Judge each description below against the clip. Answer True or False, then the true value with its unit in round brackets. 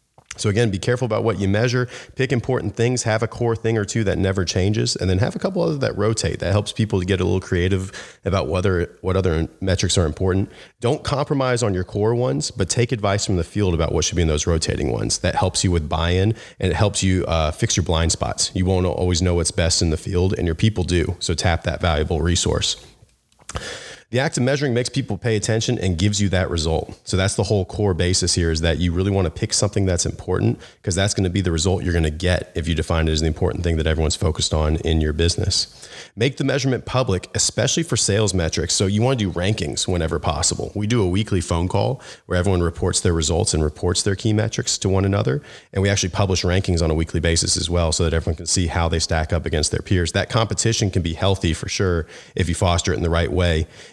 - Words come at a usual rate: False (245 wpm)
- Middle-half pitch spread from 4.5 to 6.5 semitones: False (4.0 semitones)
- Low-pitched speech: True (95 Hz)